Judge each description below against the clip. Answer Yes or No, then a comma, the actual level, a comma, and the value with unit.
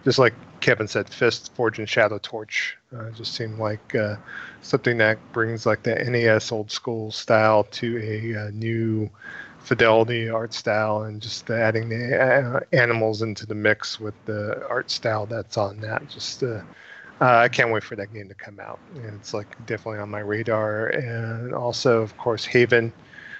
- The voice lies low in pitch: Yes, low, 110 Hz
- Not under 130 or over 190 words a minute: Yes, average, 180 wpm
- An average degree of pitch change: No, narrow, 1.3 semitones